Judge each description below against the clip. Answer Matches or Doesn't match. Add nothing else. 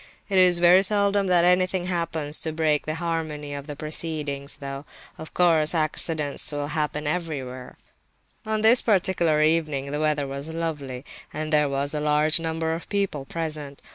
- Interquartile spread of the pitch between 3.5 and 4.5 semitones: Doesn't match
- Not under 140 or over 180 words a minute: Matches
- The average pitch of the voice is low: Doesn't match